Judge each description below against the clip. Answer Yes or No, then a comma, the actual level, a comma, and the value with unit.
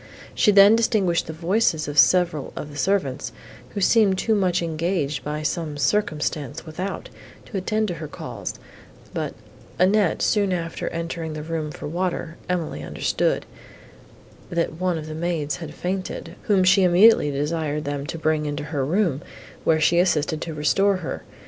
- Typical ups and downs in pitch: Yes, average, 3.6 semitones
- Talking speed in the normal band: Yes, average, 160 wpm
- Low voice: No, medium, 165 Hz